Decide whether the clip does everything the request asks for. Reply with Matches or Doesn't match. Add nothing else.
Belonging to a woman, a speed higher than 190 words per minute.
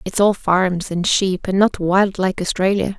Matches